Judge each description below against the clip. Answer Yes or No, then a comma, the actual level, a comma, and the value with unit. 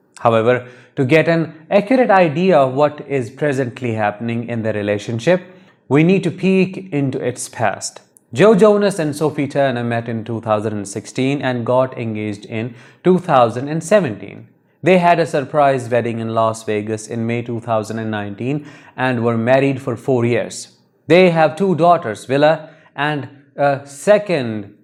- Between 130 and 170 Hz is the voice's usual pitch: Yes, low, 135 Hz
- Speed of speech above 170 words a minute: No, average, 145 wpm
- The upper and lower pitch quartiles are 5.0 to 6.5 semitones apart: Yes, average, 5.3 semitones